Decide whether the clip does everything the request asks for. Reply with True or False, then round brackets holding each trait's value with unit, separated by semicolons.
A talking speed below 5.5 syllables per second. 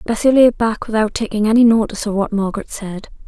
False (6.3 syllables/s)